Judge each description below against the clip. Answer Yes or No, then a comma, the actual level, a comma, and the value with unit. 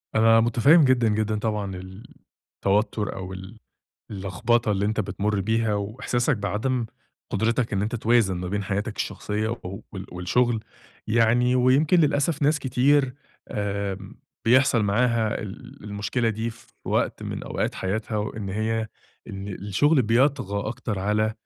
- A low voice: Yes, low, 110 Hz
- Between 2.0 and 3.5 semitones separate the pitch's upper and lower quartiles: Yes, average, 3.0 semitones